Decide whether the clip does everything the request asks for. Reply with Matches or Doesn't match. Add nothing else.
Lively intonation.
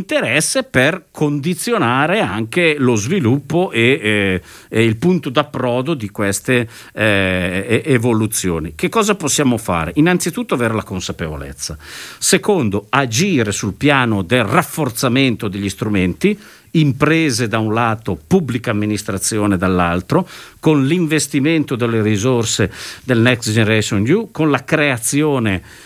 Matches